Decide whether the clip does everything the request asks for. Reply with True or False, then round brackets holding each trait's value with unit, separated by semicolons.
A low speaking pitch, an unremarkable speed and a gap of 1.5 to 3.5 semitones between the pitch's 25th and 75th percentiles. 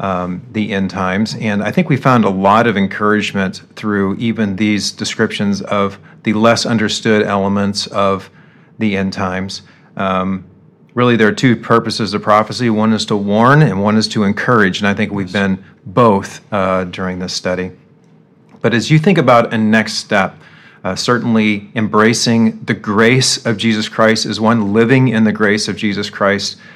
True (105 Hz; 175 wpm; 2.4 semitones)